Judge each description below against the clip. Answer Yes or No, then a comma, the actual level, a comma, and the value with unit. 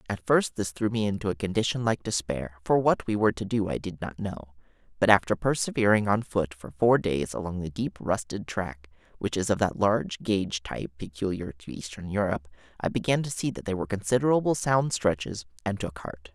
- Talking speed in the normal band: No, fast, 210 wpm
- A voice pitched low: Yes, low, 100 Hz